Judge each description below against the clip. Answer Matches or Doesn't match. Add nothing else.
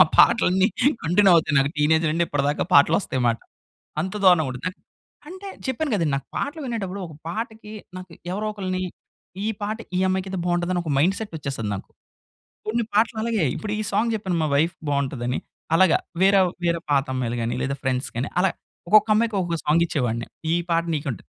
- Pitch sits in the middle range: Matches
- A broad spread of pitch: Matches